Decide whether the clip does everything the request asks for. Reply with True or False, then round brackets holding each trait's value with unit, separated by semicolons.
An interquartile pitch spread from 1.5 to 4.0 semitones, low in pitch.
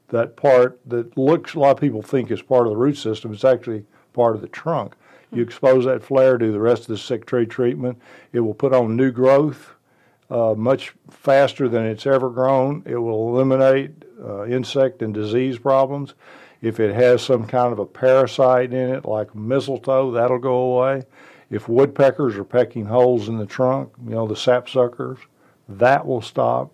True (2.4 semitones; 125 Hz)